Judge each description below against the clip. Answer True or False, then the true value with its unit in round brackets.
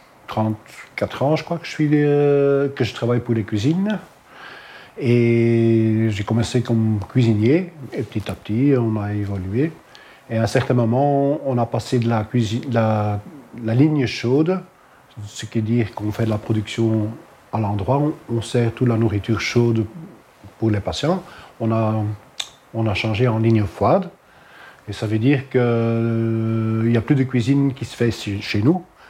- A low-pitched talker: True (115 Hz)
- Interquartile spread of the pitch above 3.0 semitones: True (3.4 semitones)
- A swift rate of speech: False (180 wpm)